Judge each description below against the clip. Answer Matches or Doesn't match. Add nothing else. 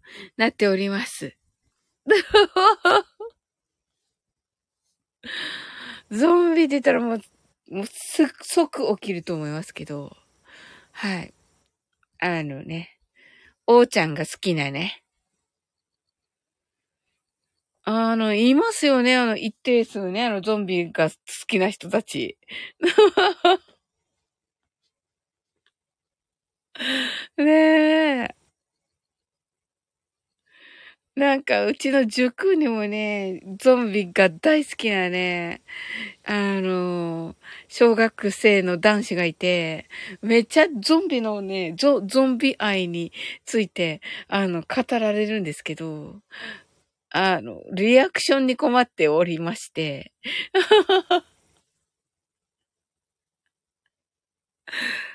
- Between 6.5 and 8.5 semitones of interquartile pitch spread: Matches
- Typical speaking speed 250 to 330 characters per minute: Doesn't match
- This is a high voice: Matches